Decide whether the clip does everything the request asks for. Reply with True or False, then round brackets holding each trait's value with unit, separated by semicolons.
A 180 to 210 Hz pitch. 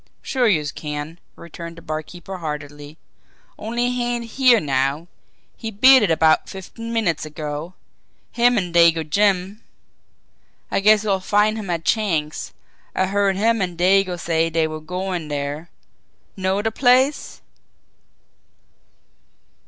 True (185 Hz)